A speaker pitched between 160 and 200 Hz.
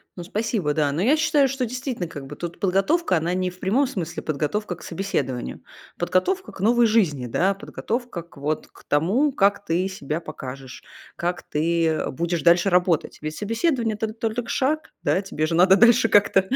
Yes: high, 190 Hz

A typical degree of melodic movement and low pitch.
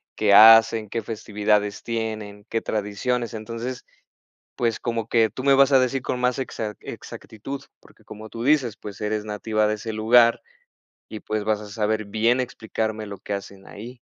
No: narrow, 1.9 semitones; low, 110 Hz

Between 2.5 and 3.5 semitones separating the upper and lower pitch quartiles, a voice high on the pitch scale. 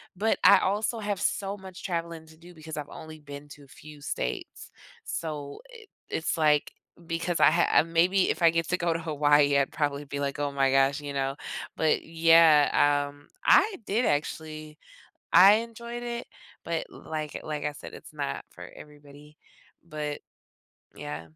No: average, 2.8 semitones; medium, 155 Hz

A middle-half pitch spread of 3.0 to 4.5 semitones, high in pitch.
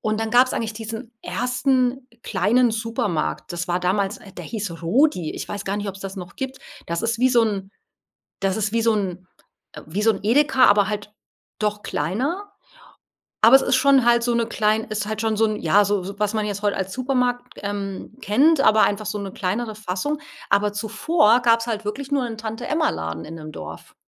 Yes: average, 3.4 semitones; high, 215 Hz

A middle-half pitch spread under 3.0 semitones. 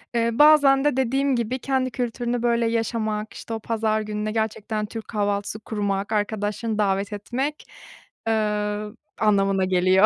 Yes: narrow, 2.4 semitones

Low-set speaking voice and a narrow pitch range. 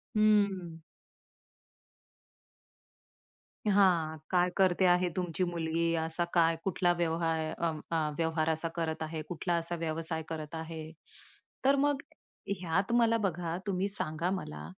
No: medium, 170 Hz; narrow, 2.3 semitones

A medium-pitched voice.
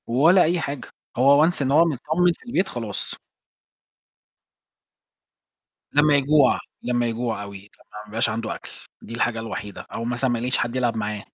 No: low, 125 Hz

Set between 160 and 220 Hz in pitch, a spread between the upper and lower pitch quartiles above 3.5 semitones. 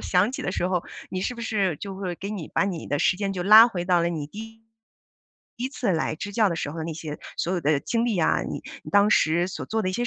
Yes: high, 190 Hz; average, 4.0 semitones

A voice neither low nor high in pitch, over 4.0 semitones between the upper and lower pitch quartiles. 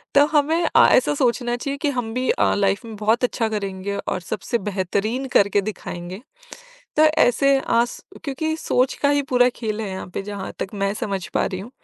No: high, 225 Hz; average, 4.7 semitones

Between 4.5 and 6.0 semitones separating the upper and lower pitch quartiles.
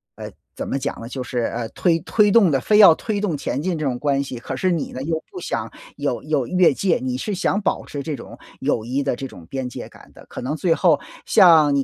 Yes: wide, 5.6 semitones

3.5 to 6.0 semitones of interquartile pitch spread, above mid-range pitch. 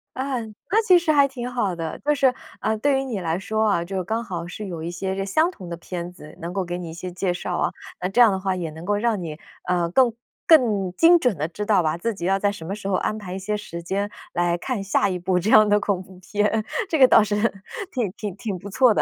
Yes: average, 4.2 semitones; high, 195 Hz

